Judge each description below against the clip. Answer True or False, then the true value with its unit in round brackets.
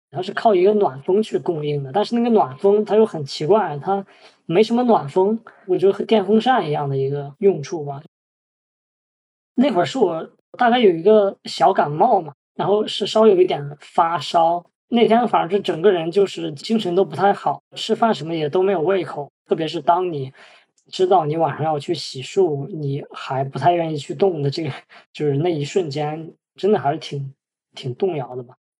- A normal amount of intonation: False (5.7 semitones)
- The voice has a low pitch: False (180 Hz)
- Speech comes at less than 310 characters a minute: True (280 characters per minute)